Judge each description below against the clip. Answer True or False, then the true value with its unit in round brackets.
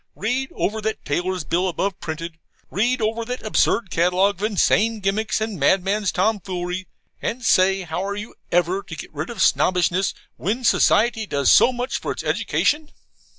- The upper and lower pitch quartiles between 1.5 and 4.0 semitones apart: True (3.6 semitones)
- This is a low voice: False (195 Hz)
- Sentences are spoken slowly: False (165 wpm)